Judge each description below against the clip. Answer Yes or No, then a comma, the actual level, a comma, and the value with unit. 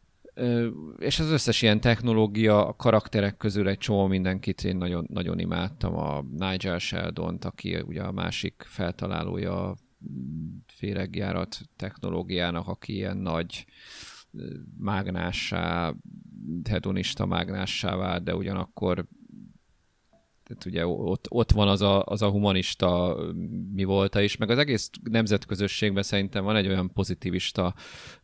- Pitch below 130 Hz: Yes, low, 100 Hz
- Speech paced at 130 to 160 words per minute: No, average, 120 wpm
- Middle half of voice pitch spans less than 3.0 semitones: Yes, narrow, 2.5 semitones